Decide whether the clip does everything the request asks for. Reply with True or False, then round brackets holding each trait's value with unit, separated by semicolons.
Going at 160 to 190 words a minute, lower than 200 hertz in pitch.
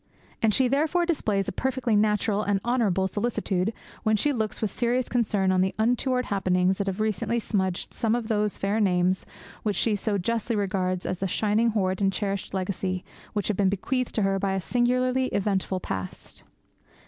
False (185 wpm; 210 Hz)